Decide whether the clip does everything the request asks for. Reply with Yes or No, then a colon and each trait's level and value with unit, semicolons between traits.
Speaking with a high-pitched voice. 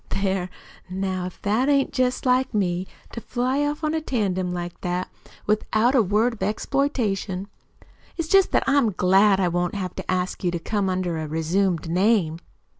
Yes: high, 195 Hz